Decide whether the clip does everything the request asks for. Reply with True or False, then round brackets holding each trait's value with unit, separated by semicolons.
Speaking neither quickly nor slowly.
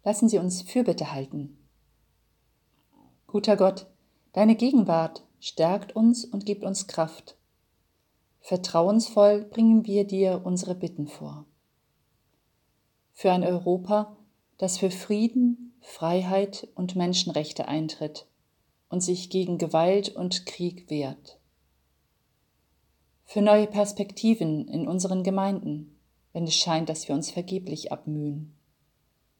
False (110 wpm)